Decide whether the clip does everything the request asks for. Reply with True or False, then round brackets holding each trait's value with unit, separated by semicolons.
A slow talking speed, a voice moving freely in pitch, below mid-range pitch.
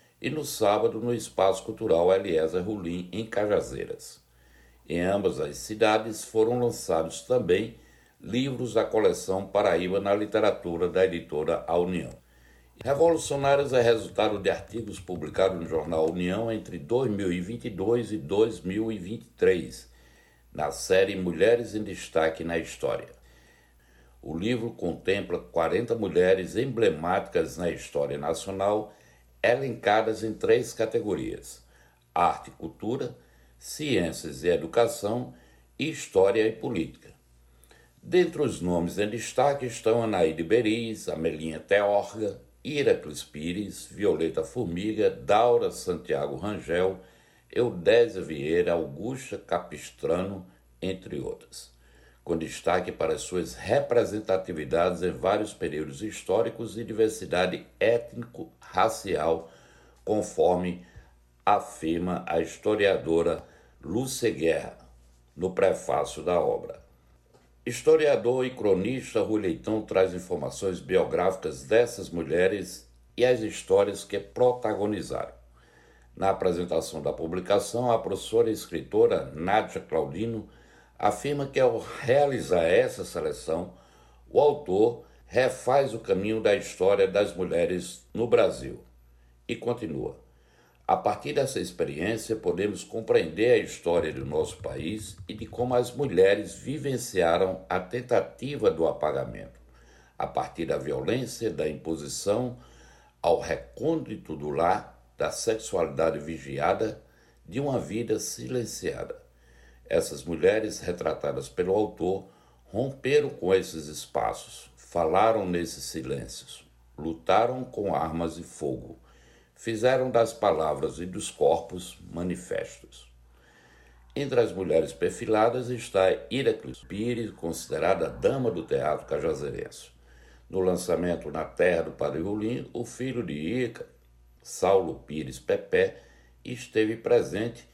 True (110 wpm; 7.5 semitones; 95 Hz)